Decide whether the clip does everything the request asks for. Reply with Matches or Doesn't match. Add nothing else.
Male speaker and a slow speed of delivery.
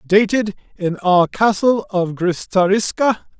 Matches